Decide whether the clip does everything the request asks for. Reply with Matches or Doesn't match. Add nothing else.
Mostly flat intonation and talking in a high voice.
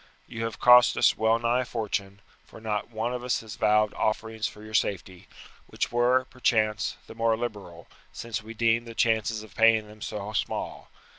Doesn't match